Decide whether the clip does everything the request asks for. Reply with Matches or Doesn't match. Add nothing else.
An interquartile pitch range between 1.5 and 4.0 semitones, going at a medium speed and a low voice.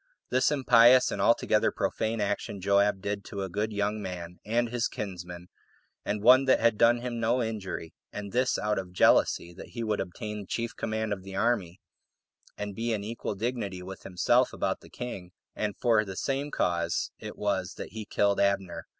Matches